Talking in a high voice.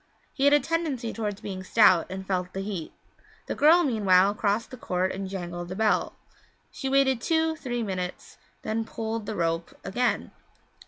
Yes: high, 210 Hz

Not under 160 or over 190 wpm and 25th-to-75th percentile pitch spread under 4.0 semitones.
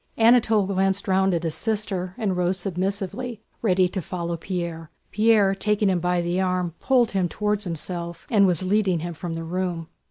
Yes: average, 180 wpm; average, 2.8 semitones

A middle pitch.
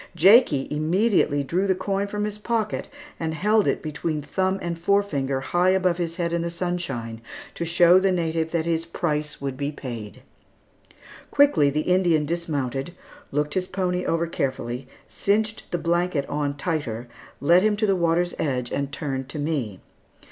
Yes: medium, 165 Hz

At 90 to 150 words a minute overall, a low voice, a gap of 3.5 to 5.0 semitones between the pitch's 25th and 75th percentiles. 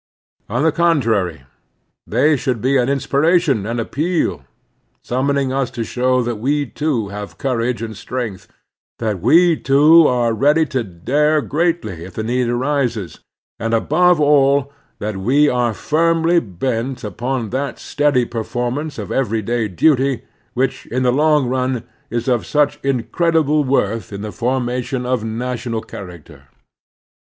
Yes: average, 140 wpm; low, 125 Hz; average, 4.1 semitones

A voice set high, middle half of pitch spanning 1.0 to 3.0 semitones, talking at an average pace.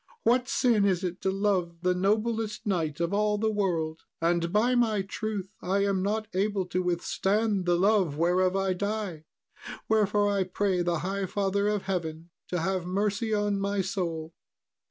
Yes: high, 195 Hz; average, 2.7 semitones; average, 170 wpm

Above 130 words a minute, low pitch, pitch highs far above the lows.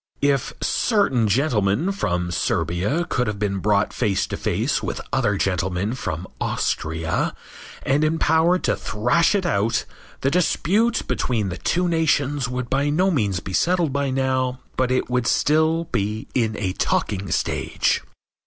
Yes: average, 150 wpm; low, 125 Hz; wide, 7.6 semitones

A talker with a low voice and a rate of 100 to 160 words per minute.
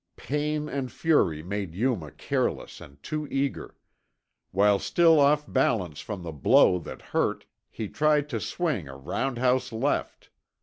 Yes: low, 125 Hz; average, 140 wpm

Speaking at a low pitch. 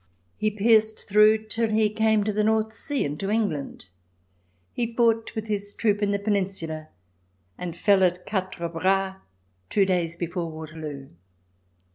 No: high, 200 Hz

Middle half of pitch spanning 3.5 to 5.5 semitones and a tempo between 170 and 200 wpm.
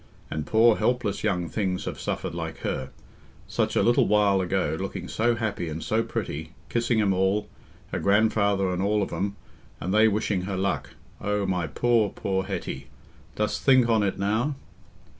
No: average, 2.8 semitones; average, 175 wpm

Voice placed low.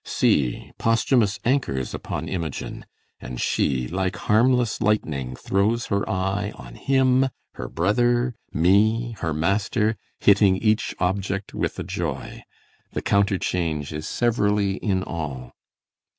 Yes: low, 100 Hz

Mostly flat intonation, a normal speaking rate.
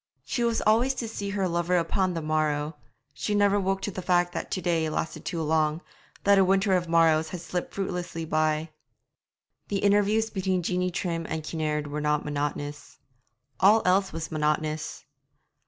No: average, 3.8 semitones; average, 170 wpm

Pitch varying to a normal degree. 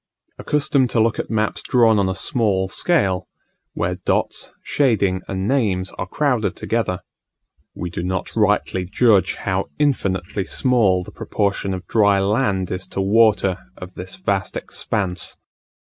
Yes: average, 3.5 semitones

